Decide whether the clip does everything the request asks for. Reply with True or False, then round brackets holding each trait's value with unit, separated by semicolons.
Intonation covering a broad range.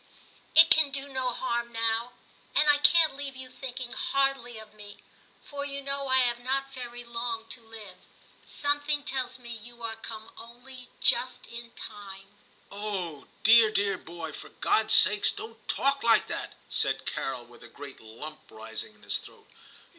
False (4.3 semitones)